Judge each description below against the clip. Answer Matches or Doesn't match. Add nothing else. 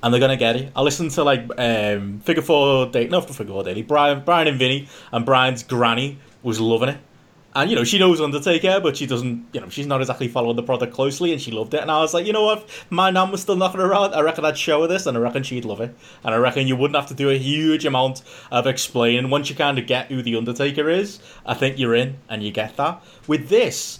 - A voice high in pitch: Doesn't match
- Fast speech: Matches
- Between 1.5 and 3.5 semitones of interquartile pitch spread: Doesn't match